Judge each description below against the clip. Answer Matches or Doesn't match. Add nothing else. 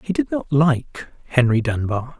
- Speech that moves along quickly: Doesn't match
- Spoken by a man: Matches